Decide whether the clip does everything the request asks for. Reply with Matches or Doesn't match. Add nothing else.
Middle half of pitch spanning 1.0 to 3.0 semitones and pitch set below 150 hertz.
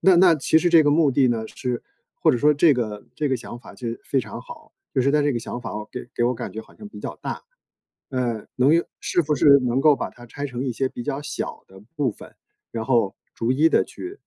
Doesn't match